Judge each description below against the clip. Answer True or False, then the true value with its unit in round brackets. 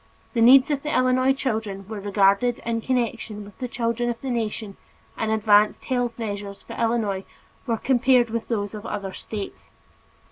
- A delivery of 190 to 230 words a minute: False (170 wpm)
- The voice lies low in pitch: False (230 Hz)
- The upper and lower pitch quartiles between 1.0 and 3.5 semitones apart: True (3.0 semitones)